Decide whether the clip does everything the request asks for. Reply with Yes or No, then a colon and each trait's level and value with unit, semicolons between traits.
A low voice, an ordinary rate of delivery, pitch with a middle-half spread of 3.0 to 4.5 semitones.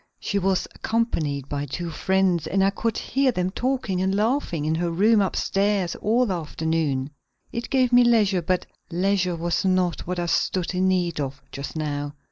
No: medium, 185 Hz; average, 180 wpm; average, 3.7 semitones